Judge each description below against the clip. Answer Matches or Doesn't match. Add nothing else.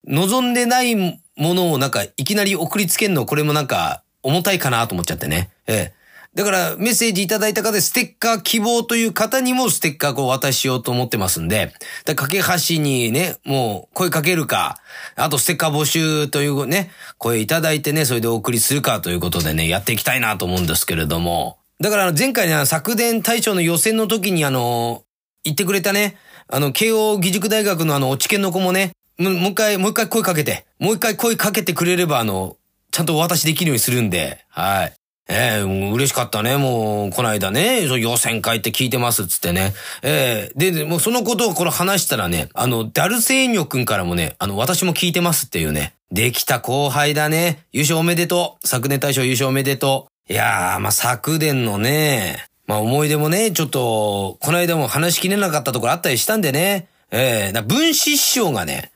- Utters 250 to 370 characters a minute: Doesn't match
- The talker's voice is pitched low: Doesn't match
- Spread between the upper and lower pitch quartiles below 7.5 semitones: Doesn't match